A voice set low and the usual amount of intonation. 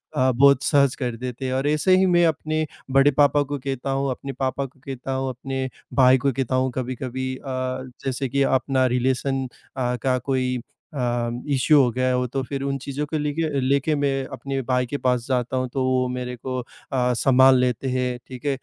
No: low, 130 Hz; narrow, 1.5 semitones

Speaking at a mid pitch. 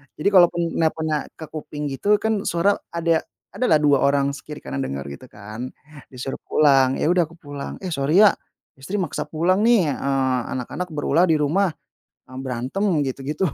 Yes: medium, 150 Hz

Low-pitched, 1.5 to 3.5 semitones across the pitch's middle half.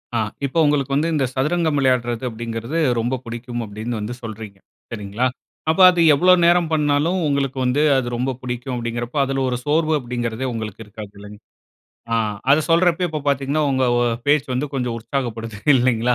No: low, 130 Hz; average, 3.9 semitones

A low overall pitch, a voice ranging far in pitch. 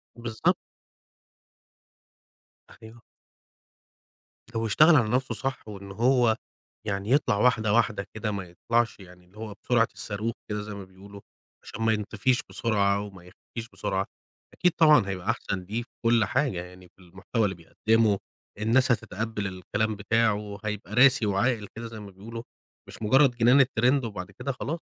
No: low, 110 Hz; average, 3.0 semitones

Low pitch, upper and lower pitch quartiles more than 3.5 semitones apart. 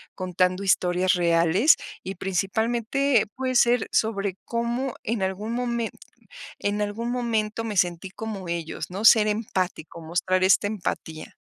No: high, 205 Hz; average, 4.0 semitones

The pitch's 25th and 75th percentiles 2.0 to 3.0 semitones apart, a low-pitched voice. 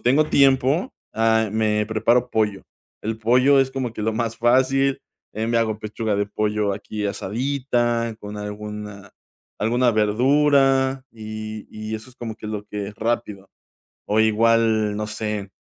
Yes: average, 2.7 semitones; low, 110 Hz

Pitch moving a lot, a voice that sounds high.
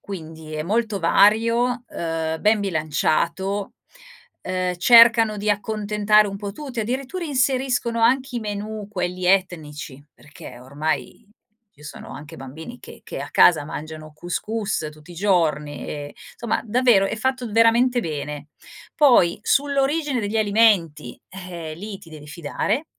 Yes: wide, 6.4 semitones; high, 200 Hz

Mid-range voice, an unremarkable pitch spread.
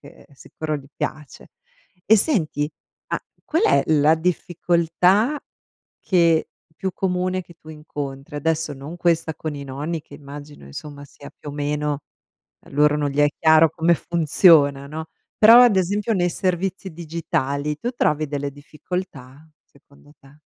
Yes: medium, 155 Hz; average, 3.5 semitones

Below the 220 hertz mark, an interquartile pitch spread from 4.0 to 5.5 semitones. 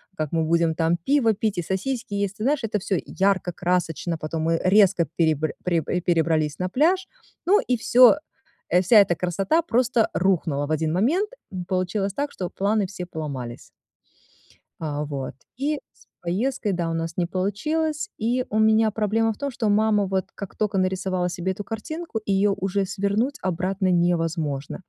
Yes: high, 190 Hz; average, 4.4 semitones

